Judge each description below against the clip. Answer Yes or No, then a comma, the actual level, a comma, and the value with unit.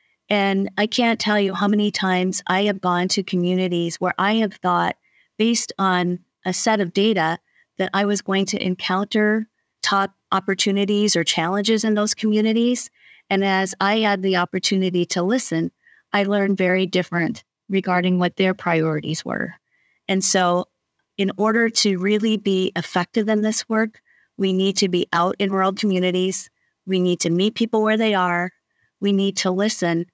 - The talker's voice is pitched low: No, high, 195 Hz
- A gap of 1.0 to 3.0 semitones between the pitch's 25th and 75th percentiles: Yes, narrow, 2.4 semitones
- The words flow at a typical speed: Yes, average, 165 wpm